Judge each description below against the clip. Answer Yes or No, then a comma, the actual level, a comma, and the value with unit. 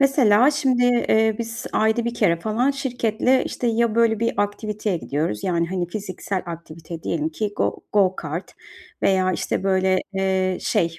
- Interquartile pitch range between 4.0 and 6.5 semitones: Yes, average, 4.4 semitones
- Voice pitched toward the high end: Yes, high, 205 Hz